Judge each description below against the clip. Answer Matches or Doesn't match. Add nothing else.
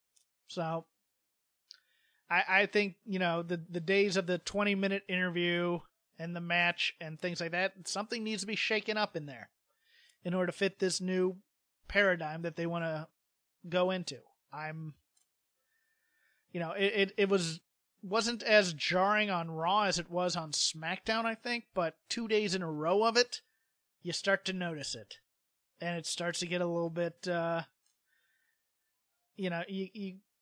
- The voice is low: Doesn't match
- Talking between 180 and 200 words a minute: Doesn't match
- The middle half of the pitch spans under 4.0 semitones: Matches